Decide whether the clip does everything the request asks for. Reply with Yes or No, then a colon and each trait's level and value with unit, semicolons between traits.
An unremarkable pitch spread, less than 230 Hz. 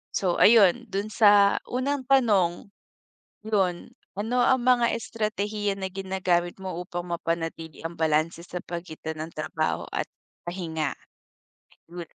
Yes: average, 3.9 semitones; medium, 185 Hz